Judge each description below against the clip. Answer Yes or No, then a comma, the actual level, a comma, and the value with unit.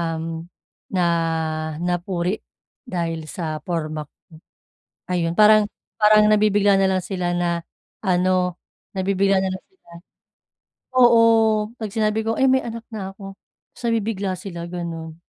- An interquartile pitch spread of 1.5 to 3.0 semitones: No, average, 3.6 semitones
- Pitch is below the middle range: No, high, 190 Hz